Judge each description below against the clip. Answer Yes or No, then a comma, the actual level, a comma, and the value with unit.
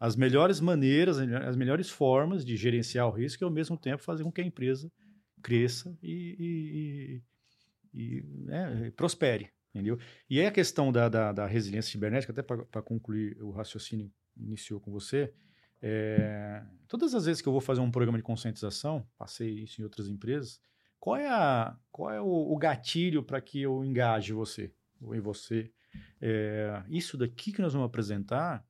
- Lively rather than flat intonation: Yes, wide, 5.8 semitones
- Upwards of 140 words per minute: Yes, average, 180 wpm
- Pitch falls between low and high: No, low, 120 Hz